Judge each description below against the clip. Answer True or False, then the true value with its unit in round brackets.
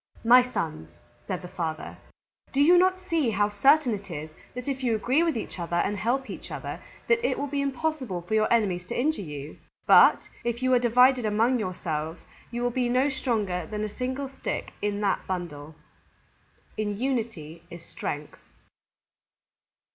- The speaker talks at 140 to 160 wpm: False (170 wpm)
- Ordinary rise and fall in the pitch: False (6.5 semitones)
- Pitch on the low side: False (225 Hz)